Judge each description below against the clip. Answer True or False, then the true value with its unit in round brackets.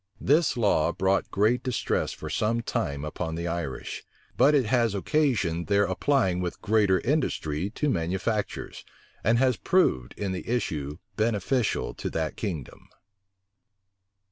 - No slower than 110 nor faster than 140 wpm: True (135 wpm)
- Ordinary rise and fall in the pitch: False (5.8 semitones)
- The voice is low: True (100 Hz)